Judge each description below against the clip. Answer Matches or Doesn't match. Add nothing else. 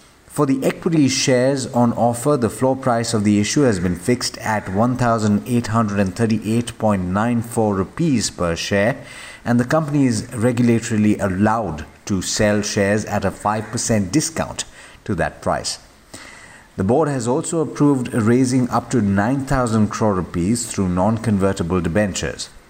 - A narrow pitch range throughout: Doesn't match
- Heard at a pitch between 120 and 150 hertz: Doesn't match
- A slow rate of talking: Matches